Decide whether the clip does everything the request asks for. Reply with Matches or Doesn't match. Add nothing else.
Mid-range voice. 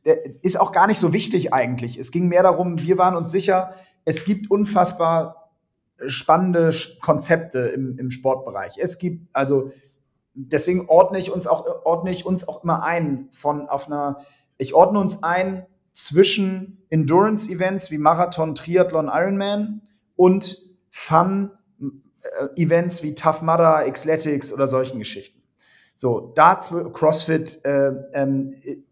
Matches